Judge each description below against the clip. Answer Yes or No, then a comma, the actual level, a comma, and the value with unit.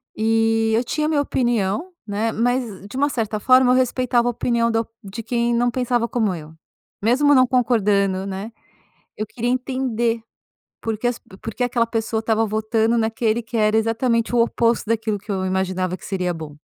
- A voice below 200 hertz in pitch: No, high, 225 Hz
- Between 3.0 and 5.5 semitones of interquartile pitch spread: No, narrow, 2.4 semitones